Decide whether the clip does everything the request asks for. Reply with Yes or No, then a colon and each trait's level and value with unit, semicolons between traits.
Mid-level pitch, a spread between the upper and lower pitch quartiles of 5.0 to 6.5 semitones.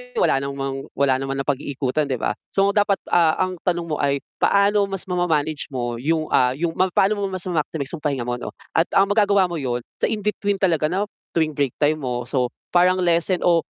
Yes: medium, 160 Hz; average, 5.3 semitones